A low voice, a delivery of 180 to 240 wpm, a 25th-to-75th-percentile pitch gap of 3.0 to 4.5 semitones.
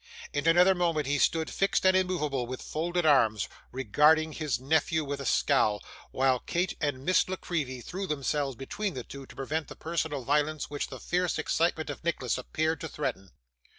No: medium, 150 Hz; average, 185 wpm; average, 3.9 semitones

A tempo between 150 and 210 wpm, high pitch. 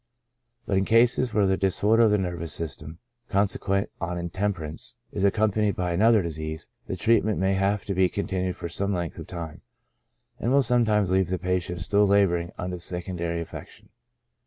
No: average, 185 wpm; very low, 95 Hz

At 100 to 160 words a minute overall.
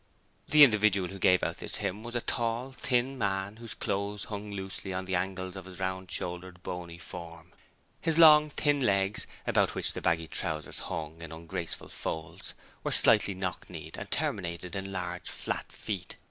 No: average, 175 wpm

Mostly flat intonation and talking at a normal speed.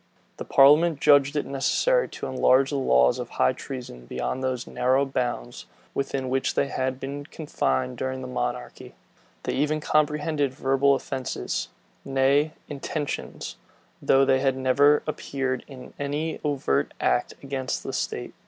Yes: narrow, 1.8 semitones; average, 145 wpm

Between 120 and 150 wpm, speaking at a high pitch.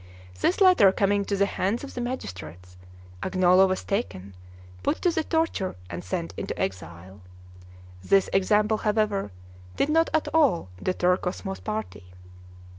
Yes: average, 140 wpm; high, 195 Hz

